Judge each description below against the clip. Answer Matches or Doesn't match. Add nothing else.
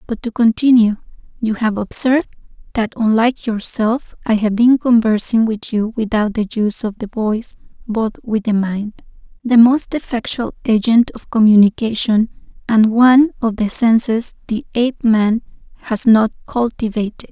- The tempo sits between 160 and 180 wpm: Doesn't match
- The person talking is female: Matches